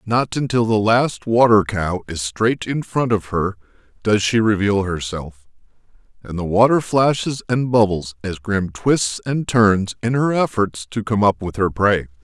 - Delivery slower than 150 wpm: No, average, 175 wpm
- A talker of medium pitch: No, low, 105 Hz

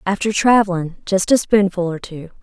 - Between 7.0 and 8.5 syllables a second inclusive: No, 5.0 syllables/s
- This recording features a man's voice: No, female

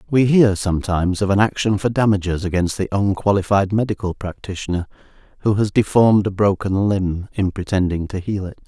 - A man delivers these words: Yes, male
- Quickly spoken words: No, average, 165 wpm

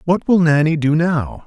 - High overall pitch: No, medium, 160 Hz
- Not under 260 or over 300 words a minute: No, fast, 205 wpm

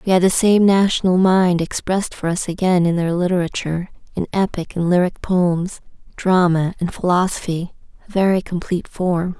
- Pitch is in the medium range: Yes, medium, 180 Hz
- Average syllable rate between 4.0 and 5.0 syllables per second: No, 5.2 syllables/s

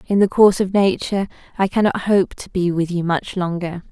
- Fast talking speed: Yes, fast, 215 wpm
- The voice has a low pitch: No, medium, 185 Hz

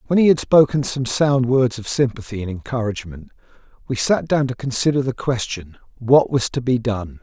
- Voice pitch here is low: Yes, low, 125 Hz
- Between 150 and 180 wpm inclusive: No, average, 190 wpm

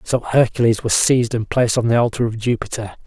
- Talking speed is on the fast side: Yes, fast, 215 wpm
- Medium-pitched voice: No, low, 115 Hz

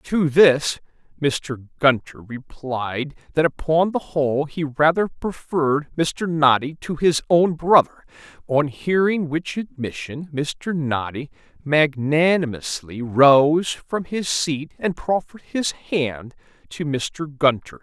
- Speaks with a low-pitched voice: No, medium, 150 Hz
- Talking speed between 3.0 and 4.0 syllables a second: Yes, 3.5 syllables/s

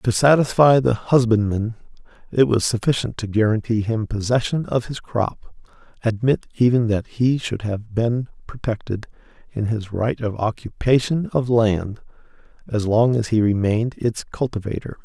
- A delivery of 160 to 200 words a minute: No, average, 145 wpm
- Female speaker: No, male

